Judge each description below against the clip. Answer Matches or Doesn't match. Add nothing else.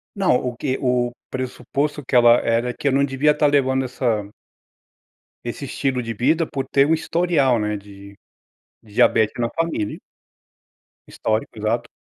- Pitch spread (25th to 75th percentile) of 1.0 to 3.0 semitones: Doesn't match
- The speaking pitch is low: Matches